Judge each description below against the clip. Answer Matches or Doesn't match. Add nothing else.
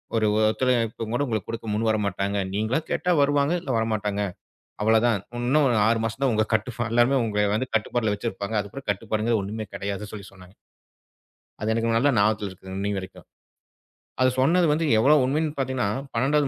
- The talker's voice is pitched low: Matches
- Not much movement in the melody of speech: Doesn't match